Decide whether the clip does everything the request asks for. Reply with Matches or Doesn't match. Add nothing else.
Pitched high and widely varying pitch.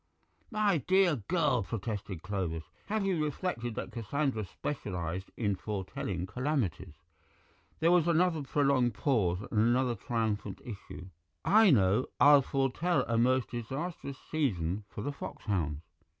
Doesn't match